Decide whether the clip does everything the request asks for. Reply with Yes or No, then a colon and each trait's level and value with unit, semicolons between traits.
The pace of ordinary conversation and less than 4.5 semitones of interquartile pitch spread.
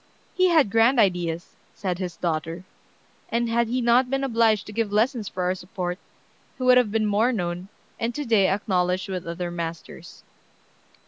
No: average, 175 wpm; average, 4.8 semitones